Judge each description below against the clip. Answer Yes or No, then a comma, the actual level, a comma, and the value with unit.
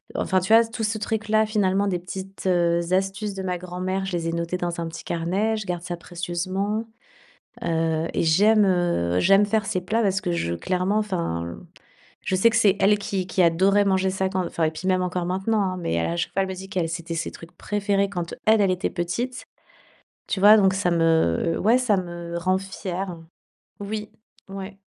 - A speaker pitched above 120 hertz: Yes, medium, 185 Hz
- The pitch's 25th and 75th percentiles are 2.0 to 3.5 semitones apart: Yes, average, 2.8 semitones